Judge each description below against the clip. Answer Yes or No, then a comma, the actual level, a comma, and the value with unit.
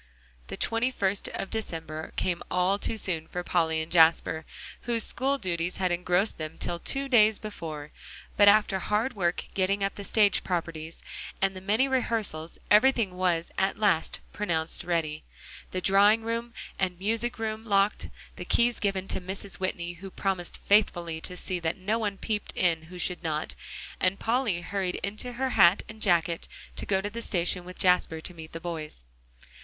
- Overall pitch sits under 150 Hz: No, high, 190 Hz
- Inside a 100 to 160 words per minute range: No, average, 175 wpm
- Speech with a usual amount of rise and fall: Yes, average, 3.8 semitones